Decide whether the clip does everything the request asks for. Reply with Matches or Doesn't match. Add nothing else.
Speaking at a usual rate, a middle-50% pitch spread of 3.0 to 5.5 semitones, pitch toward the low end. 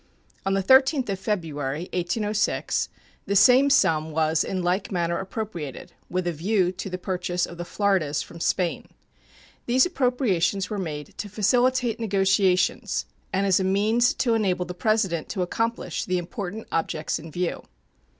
Doesn't match